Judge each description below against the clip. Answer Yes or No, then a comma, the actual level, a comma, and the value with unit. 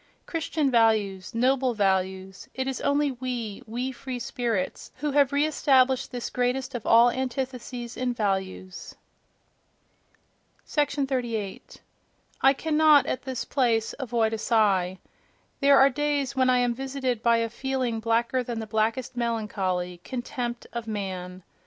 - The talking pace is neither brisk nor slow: No, slow, 130 wpm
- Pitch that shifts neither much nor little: Yes, average, 3.2 semitones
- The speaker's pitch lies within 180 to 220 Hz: No, high, 245 Hz